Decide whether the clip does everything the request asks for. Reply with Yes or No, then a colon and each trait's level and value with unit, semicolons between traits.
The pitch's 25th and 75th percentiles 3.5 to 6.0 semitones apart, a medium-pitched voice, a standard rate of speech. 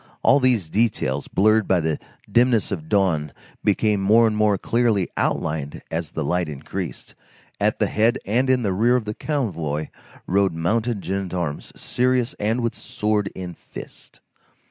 No: average, 5.2 semitones; low, 100 Hz; average, 155 wpm